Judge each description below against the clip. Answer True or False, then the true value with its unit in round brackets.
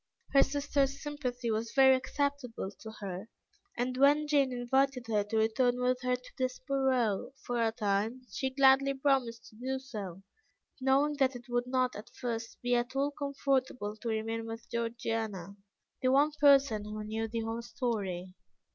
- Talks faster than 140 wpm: True (165 wpm)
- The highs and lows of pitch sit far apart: False (3.2 semitones)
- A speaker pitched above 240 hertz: True (250 Hz)